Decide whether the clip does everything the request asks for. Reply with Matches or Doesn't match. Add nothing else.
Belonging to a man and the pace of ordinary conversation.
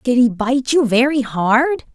Doesn't match